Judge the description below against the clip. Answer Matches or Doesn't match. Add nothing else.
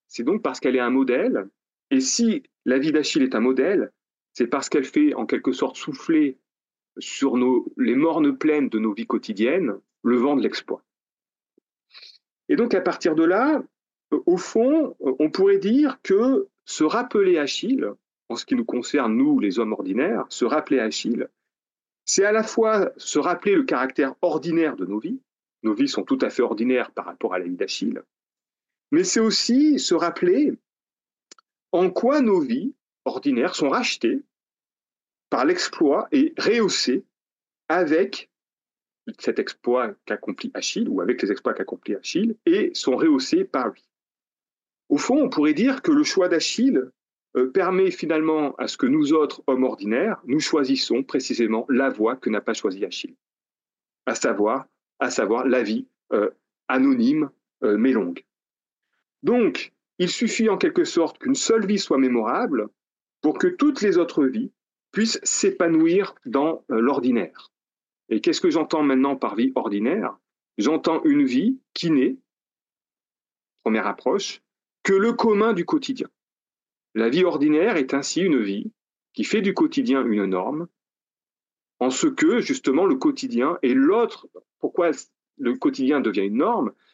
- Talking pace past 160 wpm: Doesn't match